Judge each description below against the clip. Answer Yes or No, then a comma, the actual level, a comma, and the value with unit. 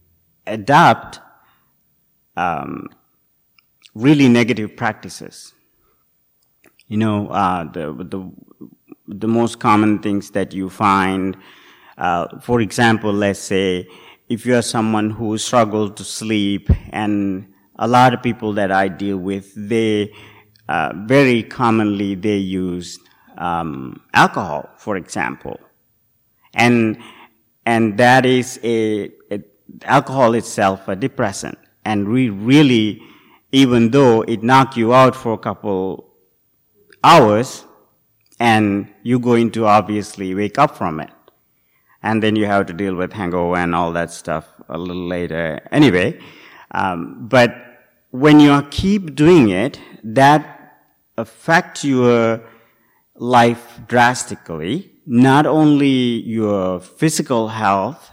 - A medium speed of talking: No, slow, 120 wpm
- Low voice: Yes, low, 110 Hz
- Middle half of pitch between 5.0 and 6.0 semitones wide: No, average, 3.6 semitones